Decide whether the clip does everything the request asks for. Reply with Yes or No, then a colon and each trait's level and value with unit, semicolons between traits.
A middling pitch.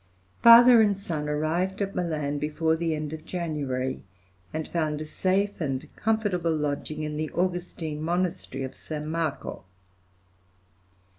Yes: medium, 160 Hz